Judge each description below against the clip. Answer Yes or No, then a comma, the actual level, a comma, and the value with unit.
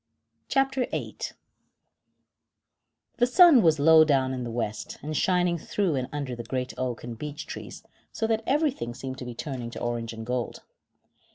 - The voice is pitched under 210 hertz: Yes, medium, 140 Hz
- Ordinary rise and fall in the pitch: No, wide, 7.0 semitones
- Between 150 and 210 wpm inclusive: Yes, average, 170 wpm